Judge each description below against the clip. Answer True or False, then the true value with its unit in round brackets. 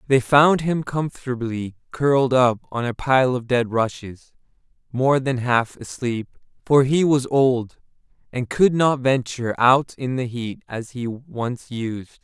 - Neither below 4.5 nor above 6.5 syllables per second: False (3.9 syllables/s)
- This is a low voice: True (125 Hz)